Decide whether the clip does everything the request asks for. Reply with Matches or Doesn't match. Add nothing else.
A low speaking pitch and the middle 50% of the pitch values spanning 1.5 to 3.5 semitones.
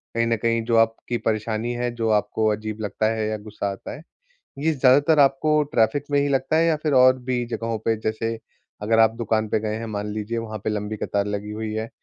Matches